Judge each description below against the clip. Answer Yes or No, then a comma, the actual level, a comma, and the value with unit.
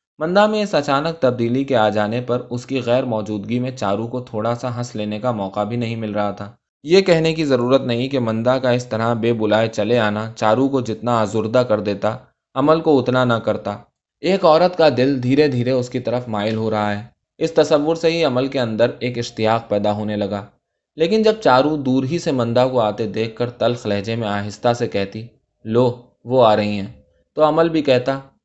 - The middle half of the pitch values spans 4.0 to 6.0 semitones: No, average, 3.6 semitones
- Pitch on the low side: Yes, low, 120 Hz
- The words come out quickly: Yes, fast, 215 wpm